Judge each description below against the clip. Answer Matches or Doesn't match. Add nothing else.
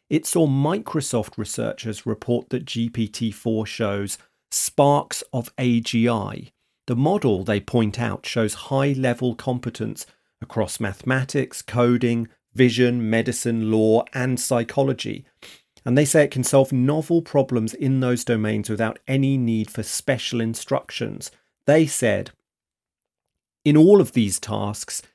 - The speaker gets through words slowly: Matches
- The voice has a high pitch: Doesn't match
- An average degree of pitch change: Matches